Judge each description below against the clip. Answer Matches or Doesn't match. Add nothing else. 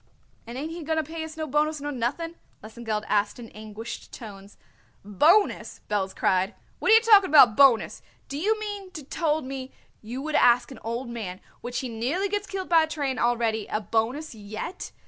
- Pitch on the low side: Doesn't match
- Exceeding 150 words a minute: Matches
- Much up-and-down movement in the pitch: Matches